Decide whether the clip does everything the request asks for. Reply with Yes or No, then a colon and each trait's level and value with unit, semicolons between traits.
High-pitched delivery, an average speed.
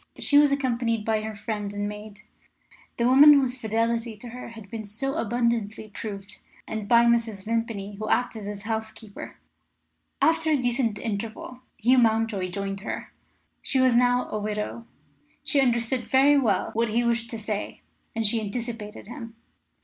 Yes: high, 230 Hz; average, 160 wpm